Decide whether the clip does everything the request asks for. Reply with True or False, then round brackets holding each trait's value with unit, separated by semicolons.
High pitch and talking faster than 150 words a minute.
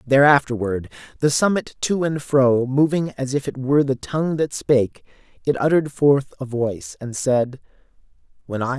False (135 Hz; 165 wpm)